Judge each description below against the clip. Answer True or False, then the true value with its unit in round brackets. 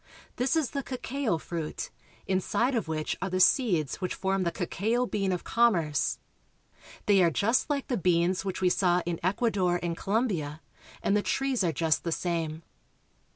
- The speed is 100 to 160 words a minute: False (170 wpm)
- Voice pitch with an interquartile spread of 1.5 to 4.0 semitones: False (5.3 semitones)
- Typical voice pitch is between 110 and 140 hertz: False (185 Hz)